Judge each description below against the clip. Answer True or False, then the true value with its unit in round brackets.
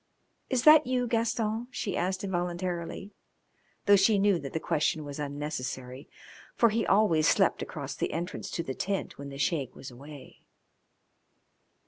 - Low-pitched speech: False (175 Hz)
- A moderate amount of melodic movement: False (6.5 semitones)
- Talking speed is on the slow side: False (150 wpm)